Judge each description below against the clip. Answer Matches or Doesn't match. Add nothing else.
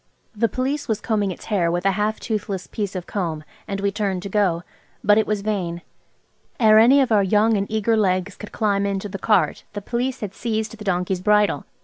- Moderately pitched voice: Doesn't match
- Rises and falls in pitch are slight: Matches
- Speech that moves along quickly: Matches